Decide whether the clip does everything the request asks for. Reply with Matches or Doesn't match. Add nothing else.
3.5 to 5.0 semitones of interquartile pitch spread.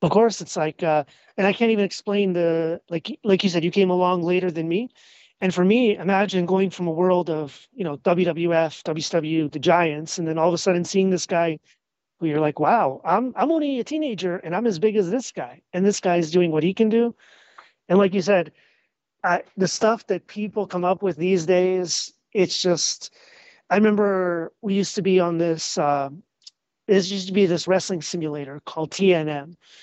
Doesn't match